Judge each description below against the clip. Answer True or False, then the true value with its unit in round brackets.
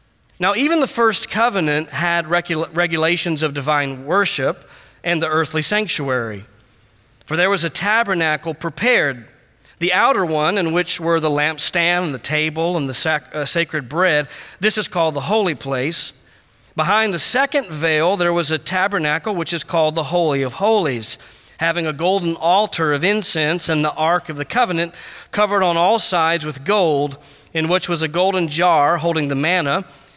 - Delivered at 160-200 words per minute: True (170 wpm)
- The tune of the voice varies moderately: True (3.5 semitones)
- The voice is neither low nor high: True (165 Hz)